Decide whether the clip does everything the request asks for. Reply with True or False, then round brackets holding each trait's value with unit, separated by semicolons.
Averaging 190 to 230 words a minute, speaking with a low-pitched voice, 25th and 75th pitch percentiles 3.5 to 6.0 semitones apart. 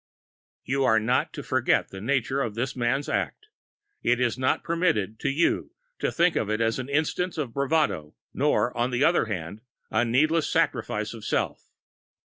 False (175 wpm; 125 Hz; 4.6 semitones)